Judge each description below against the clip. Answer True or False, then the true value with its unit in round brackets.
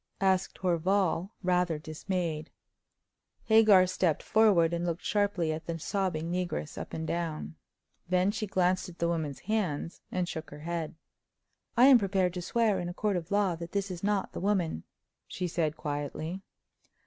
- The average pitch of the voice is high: False (180 Hz)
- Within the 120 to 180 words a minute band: True (165 wpm)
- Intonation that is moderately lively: True (3.0 semitones)